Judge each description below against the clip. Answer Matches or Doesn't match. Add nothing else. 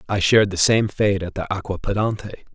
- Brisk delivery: Doesn't match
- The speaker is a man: Matches